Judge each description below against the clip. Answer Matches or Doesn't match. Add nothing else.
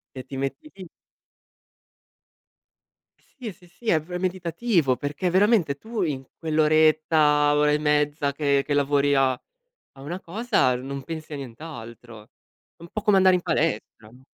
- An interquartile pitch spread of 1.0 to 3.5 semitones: Doesn't match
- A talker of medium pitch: Matches